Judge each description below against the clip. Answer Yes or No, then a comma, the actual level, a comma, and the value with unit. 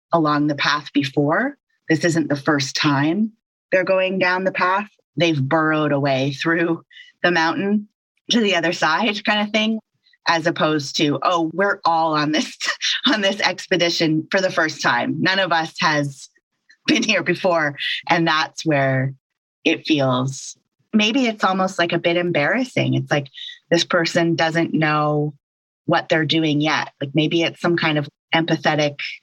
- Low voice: No, medium, 165 Hz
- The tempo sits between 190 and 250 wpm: No, average, 160 wpm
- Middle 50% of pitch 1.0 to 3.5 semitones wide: No, average, 4.0 semitones